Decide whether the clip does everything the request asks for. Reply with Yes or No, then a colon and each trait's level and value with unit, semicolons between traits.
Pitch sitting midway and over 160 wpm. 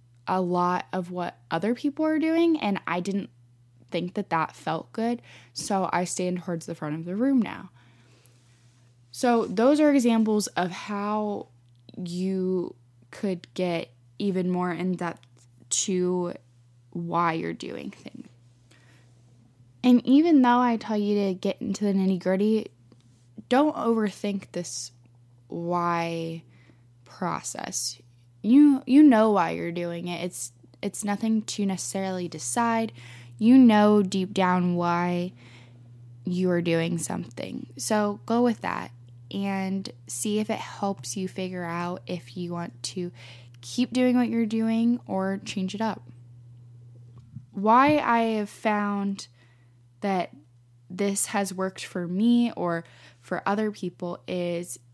No: medium, 180 Hz; slow, 135 wpm